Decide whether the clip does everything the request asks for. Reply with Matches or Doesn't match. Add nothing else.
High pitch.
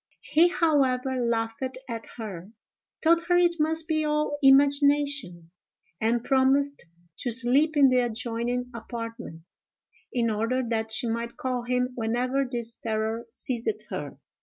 Matches